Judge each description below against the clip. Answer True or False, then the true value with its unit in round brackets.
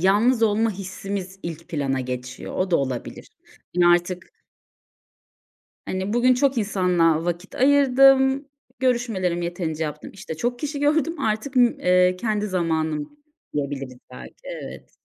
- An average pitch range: False (6.7 semitones)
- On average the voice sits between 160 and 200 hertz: True (190 Hz)